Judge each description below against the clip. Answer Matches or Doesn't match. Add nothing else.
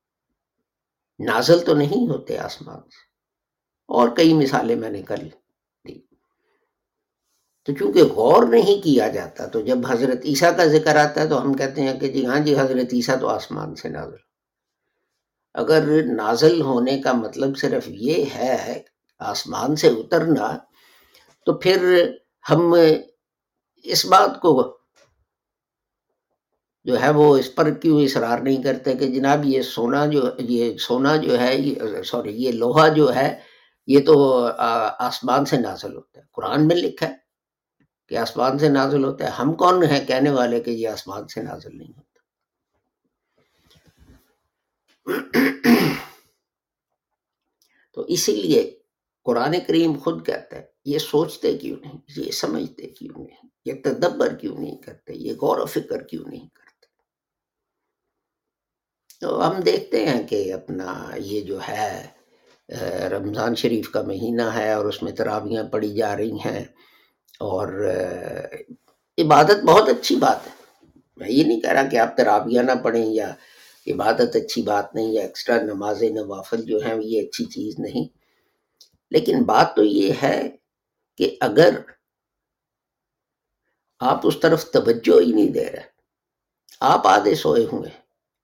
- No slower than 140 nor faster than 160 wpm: Matches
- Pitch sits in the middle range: Matches